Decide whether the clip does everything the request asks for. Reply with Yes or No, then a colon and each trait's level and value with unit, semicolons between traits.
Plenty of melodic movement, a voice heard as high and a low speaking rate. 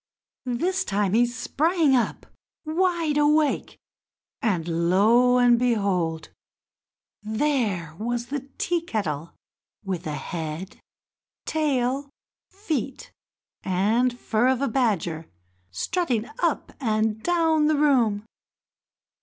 Yes: wide, 6.8 semitones; high, 240 Hz; slow, 100 wpm